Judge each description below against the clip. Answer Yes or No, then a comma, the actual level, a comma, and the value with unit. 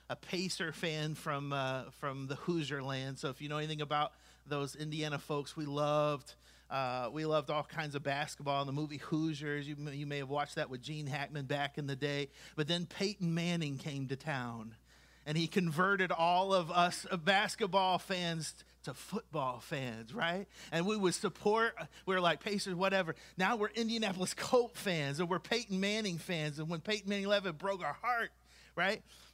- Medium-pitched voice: Yes, medium, 155 Hz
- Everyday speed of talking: Yes, average, 190 wpm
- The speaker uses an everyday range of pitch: Yes, average, 4.5 semitones